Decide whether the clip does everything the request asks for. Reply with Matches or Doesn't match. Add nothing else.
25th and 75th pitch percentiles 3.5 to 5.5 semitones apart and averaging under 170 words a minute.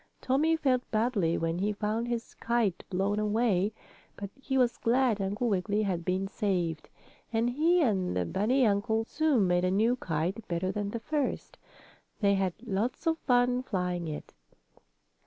Matches